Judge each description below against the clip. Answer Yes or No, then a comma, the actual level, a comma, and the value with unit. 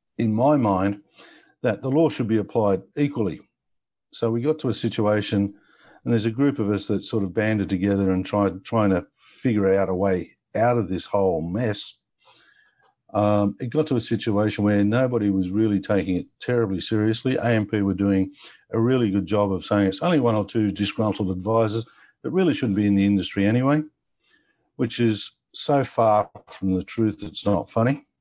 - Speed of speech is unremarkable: Yes, average, 185 wpm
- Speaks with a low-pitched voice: Yes, low, 105 Hz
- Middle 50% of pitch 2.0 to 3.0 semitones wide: Yes, average, 2.7 semitones